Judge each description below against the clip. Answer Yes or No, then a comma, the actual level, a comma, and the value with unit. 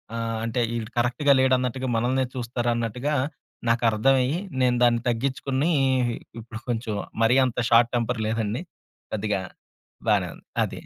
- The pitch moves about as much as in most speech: No, narrow, 2.1 semitones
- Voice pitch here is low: Yes, low, 120 Hz